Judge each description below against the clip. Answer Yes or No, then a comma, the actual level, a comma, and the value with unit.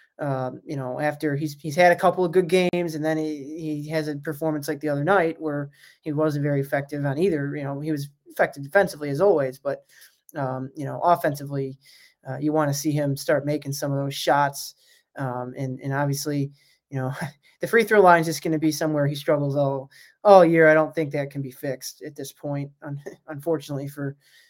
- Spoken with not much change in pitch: Yes, narrow, 2.2 semitones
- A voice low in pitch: No, medium, 145 Hz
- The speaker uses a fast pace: Yes, fast, 215 wpm